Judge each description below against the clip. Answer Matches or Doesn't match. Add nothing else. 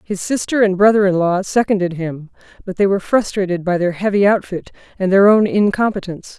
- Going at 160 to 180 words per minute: Doesn't match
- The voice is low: Doesn't match